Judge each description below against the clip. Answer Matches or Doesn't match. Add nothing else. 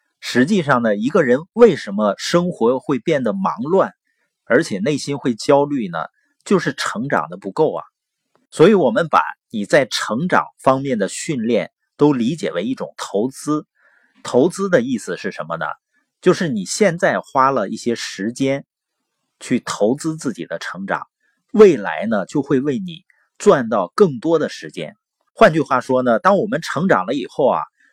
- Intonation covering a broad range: Matches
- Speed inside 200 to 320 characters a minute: Matches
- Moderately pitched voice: Matches